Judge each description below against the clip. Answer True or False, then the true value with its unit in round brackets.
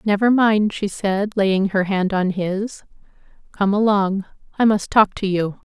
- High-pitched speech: True (200 Hz)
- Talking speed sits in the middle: True (170 wpm)